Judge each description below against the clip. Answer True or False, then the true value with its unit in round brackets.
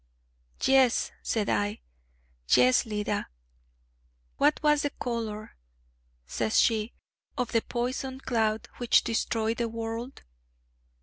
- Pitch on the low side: False (230 Hz)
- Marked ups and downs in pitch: False (2.7 semitones)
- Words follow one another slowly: True (105 wpm)